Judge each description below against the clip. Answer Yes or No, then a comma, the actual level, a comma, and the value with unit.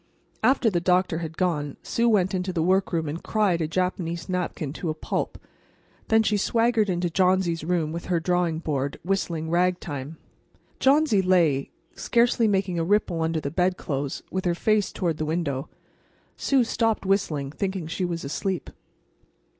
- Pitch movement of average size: Yes, average, 3.1 semitones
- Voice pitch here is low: No, medium, 180 Hz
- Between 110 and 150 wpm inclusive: No, average, 160 wpm